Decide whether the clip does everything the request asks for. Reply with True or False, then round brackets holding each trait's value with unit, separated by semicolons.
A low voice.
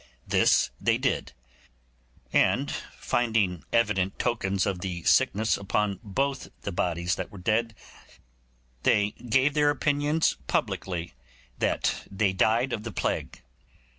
True (105 Hz)